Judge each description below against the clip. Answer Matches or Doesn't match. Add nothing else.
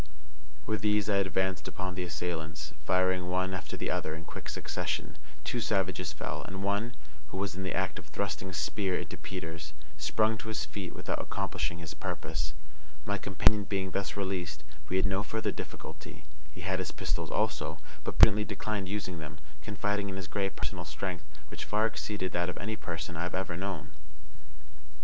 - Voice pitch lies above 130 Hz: Doesn't match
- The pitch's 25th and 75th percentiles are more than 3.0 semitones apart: Doesn't match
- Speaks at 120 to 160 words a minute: Doesn't match